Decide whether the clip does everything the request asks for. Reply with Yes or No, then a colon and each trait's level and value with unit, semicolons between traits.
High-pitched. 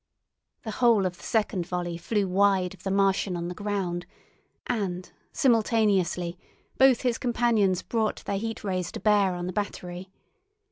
Yes: high, 195 Hz